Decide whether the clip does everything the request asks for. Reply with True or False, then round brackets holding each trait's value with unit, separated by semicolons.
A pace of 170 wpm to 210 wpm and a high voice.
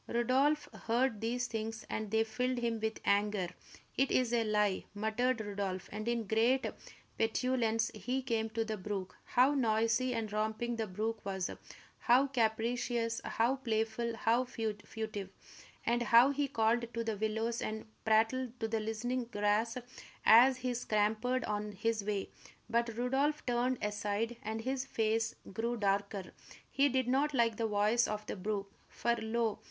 False (155 wpm; 225 Hz)